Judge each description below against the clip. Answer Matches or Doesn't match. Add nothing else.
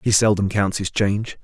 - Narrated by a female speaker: Doesn't match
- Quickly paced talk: Matches